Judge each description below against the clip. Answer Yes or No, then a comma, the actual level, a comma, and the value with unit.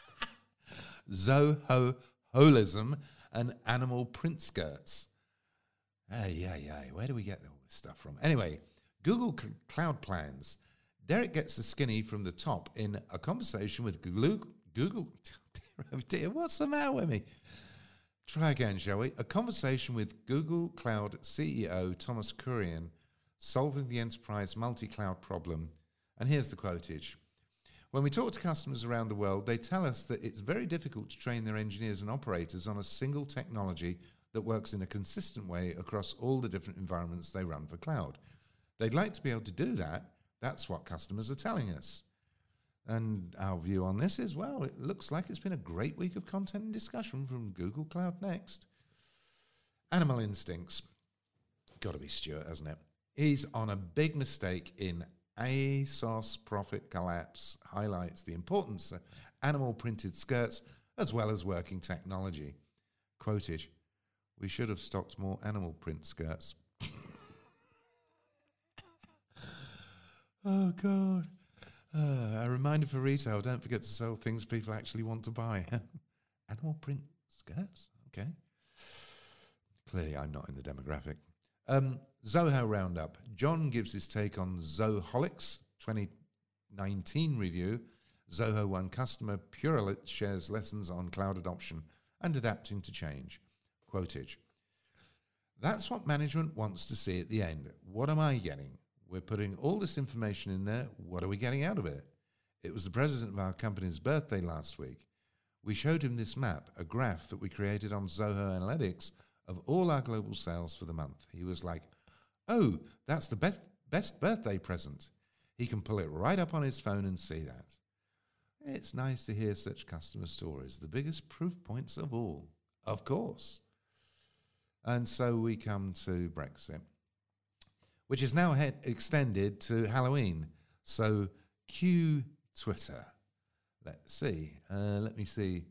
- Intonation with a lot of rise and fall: Yes, wide, 6.4 semitones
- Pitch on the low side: Yes, low, 105 Hz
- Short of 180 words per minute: Yes, average, 155 wpm